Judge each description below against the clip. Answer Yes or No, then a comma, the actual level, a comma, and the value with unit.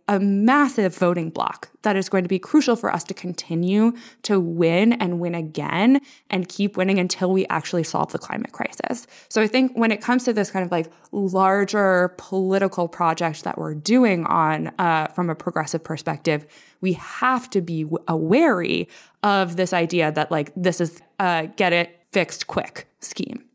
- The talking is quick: No, average, 180 wpm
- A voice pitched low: No, medium, 185 Hz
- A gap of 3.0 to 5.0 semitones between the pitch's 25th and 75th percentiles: Yes, average, 3.4 semitones